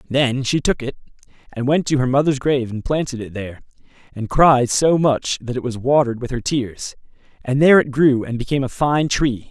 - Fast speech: Yes, fast, 215 wpm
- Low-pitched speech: Yes, low, 130 Hz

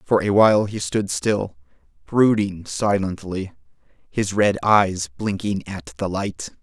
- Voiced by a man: Yes, male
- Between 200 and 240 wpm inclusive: No, slow, 135 wpm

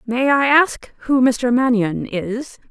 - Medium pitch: No, very high, 250 Hz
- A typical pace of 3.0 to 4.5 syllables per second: Yes, 3.4 syllables/s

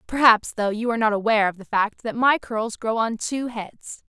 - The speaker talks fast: Yes, fast, 235 wpm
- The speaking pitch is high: Yes, high, 225 Hz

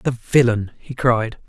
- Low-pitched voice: Yes, low, 120 Hz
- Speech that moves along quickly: No, average, 160 wpm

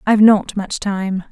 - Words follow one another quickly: No, average, 185 wpm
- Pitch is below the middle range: No, high, 200 Hz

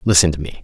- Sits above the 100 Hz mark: No, very low, 85 Hz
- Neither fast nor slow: No, fast, 285 wpm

